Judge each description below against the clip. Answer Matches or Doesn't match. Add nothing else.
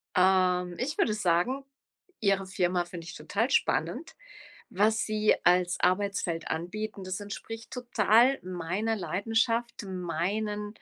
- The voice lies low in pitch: Doesn't match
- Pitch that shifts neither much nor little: Matches